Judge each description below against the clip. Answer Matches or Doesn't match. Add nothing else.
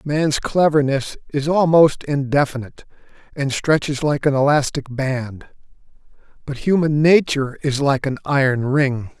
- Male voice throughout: Matches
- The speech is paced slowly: Matches